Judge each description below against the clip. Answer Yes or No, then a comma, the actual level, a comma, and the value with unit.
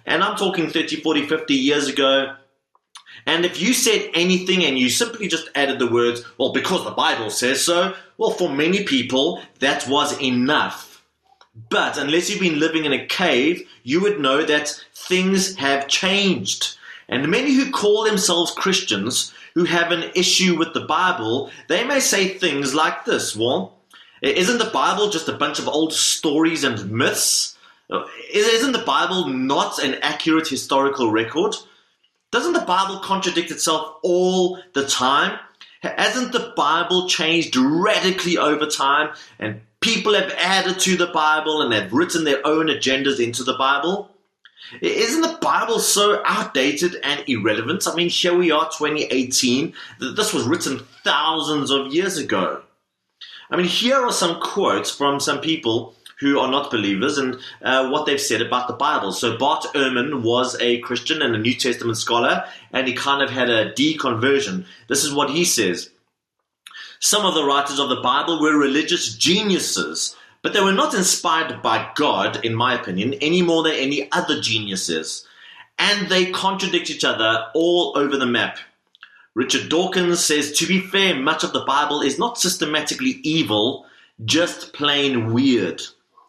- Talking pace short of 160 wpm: No, average, 165 wpm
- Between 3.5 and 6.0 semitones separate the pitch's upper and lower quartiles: Yes, average, 5.2 semitones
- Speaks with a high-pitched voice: No, medium, 160 Hz